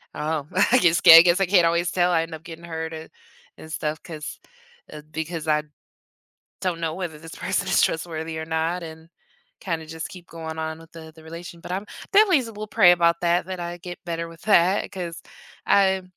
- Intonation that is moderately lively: No, narrow, 1.7 semitones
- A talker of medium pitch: Yes, medium, 165 Hz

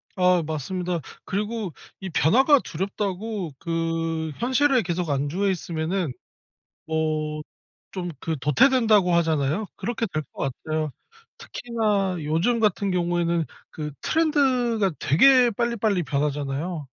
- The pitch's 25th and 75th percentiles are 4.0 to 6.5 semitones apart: Yes, wide, 5.6 semitones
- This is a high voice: No, medium, 180 Hz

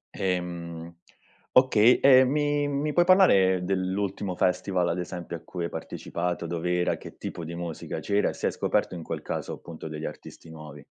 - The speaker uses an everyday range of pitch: Yes, average, 3.6 semitones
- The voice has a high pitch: No, very low, 90 Hz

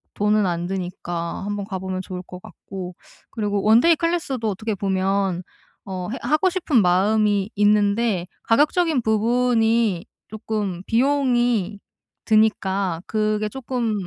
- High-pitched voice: Yes, high, 210 Hz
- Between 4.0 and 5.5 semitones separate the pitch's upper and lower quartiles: No, average, 3.6 semitones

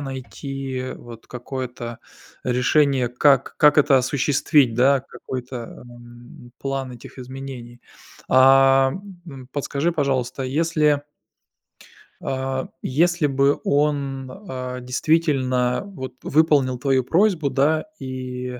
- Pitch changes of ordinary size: No, narrow, 2.2 semitones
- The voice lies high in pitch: No, low, 135 Hz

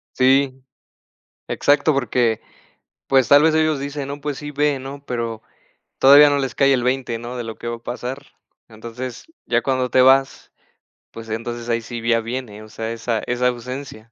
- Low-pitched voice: Yes, low, 125 Hz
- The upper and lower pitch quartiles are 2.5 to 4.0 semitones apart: Yes, average, 2.9 semitones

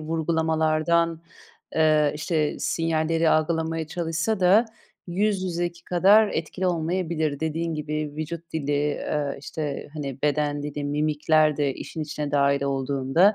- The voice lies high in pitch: No, medium, 155 Hz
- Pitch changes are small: Yes, narrow, 2.2 semitones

